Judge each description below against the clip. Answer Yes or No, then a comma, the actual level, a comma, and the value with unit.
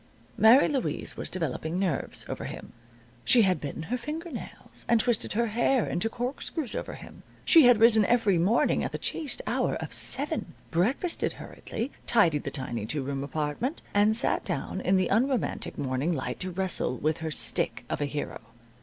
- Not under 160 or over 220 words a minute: Yes, average, 180 wpm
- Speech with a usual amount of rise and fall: No, wide, 7.5 semitones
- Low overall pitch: No, high, 205 Hz